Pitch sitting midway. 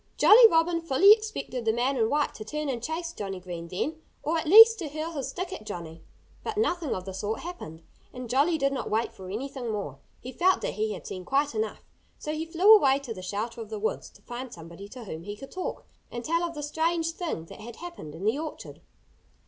No: very high, 265 Hz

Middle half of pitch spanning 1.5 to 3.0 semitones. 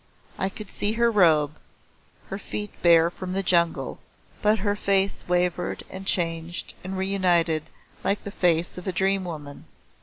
Yes: narrow, 2.5 semitones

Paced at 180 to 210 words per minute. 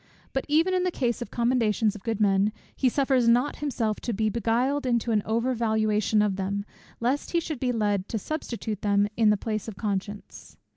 Yes: fast, 205 wpm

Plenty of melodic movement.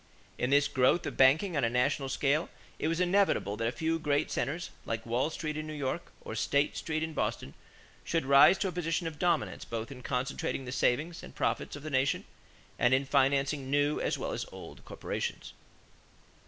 No: average, 3.4 semitones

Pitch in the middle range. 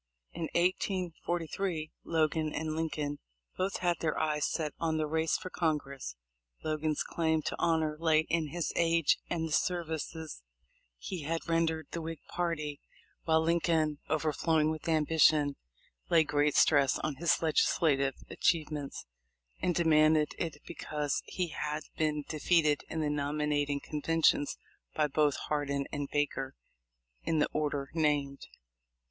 Yes: medium, 155 Hz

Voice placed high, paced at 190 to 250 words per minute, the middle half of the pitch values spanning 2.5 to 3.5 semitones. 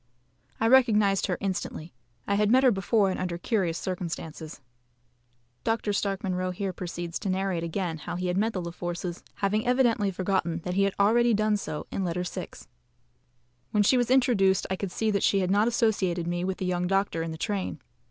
Yes: high, 195 Hz; average, 200 wpm; average, 2.9 semitones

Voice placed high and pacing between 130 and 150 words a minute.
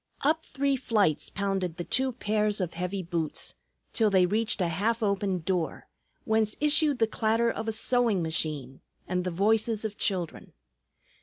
No: high, 205 Hz; average, 160 wpm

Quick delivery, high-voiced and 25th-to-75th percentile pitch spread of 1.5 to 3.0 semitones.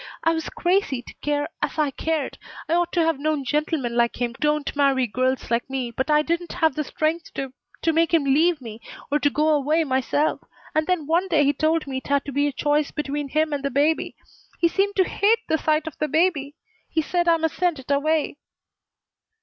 Yes: fast, 220 wpm; very high, 300 Hz; average, 2.7 semitones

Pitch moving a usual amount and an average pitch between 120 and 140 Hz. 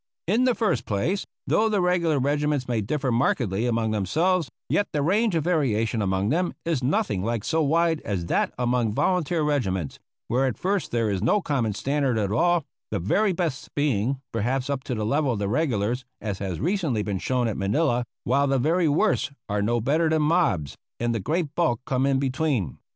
No: wide, 6.5 semitones; low, 135 Hz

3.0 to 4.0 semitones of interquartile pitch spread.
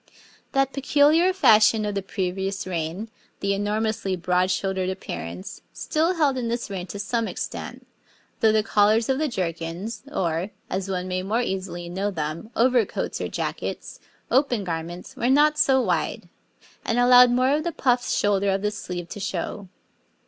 No: average, 5.0 semitones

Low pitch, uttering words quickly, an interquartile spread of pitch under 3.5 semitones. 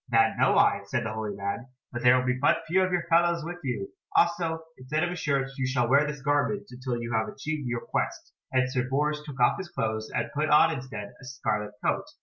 No: low, 130 Hz; fast, 235 wpm; average, 4.3 semitones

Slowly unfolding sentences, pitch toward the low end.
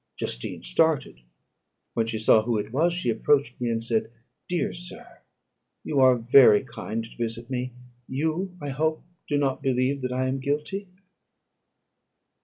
No: average, 155 wpm; low, 130 Hz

